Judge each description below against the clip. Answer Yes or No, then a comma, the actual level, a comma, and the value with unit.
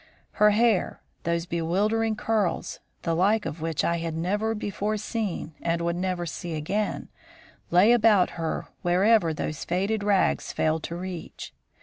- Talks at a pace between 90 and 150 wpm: Yes, average, 145 wpm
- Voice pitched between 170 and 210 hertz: Yes, medium, 185 Hz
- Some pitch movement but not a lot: Yes, average, 4.0 semitones